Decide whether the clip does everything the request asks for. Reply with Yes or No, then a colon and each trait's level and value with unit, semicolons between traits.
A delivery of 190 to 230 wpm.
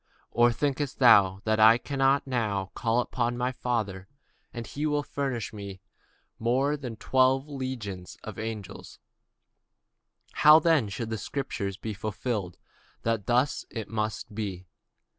No: average, 140 wpm